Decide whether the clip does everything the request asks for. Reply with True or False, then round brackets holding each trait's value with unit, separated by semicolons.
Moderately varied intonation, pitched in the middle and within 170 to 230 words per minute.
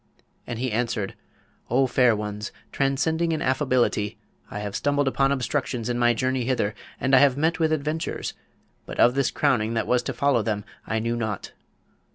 False (3.7 semitones; 125 Hz; 180 wpm)